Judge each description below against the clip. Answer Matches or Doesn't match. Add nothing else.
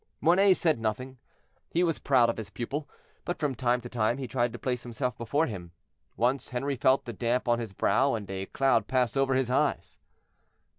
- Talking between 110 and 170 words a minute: Doesn't match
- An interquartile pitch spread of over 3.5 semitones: Doesn't match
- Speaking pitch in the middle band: Doesn't match